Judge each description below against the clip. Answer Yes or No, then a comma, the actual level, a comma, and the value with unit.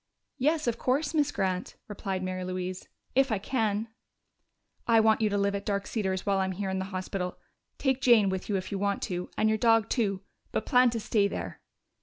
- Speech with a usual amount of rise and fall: Yes, average, 3.5 semitones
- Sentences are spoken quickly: Yes, fast, 210 wpm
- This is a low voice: No, high, 205 Hz